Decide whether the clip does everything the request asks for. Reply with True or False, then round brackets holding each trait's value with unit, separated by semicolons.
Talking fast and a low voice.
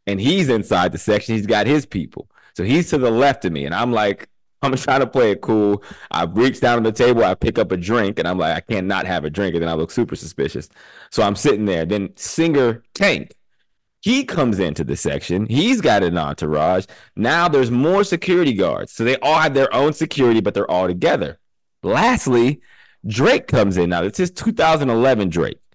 True (210 wpm; 115 Hz)